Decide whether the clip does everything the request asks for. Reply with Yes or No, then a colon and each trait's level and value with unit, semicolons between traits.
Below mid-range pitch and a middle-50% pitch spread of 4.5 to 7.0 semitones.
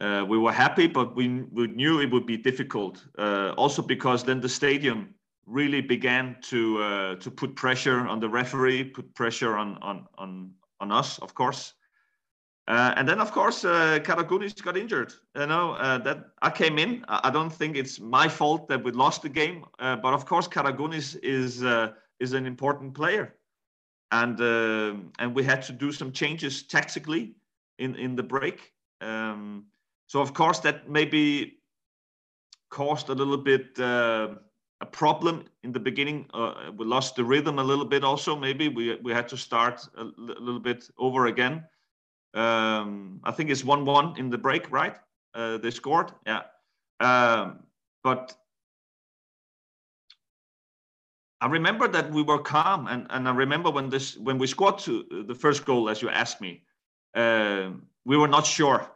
No: low, 130 Hz; average, 3.7 semitones